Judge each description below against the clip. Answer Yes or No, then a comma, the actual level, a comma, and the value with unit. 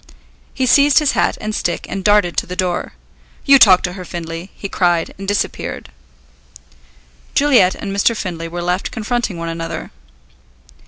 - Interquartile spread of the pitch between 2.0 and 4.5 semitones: Yes, average, 3.6 semitones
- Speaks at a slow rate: No, average, 160 wpm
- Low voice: No, medium, 185 Hz